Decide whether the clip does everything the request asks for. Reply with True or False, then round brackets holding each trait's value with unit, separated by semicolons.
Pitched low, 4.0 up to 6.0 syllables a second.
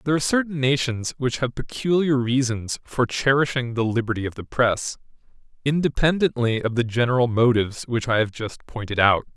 True (125 Hz; 5.5 syllables/s)